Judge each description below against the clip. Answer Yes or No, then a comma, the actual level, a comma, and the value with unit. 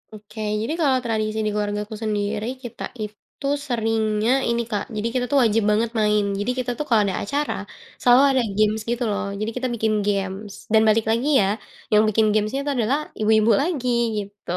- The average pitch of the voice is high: Yes, high, 220 Hz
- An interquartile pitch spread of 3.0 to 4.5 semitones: No, narrow, 2.4 semitones